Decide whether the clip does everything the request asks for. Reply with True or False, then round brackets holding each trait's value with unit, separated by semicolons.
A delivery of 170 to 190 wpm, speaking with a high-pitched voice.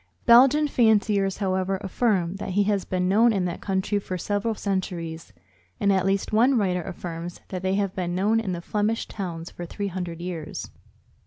True (180 wpm; 195 Hz)